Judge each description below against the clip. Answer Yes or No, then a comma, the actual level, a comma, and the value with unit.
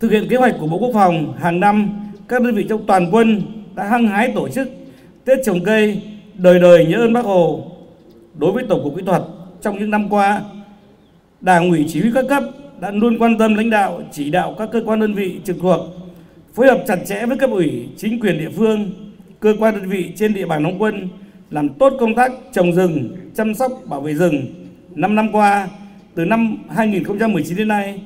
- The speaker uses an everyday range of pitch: Yes, average, 3.7 semitones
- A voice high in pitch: Yes, high, 200 Hz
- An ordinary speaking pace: Yes, average, 215 wpm